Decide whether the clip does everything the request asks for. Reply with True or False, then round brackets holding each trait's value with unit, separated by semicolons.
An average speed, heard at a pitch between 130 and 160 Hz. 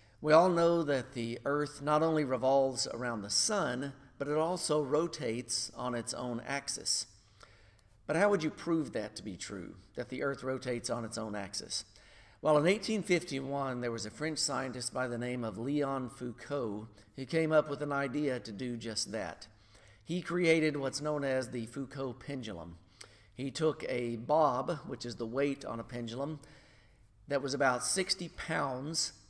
True (175 wpm; 135 Hz)